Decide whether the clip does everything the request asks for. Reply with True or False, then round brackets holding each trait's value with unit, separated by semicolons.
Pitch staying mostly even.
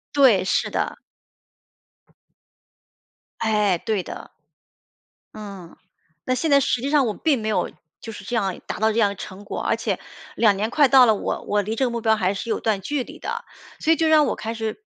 False (3.9 semitones)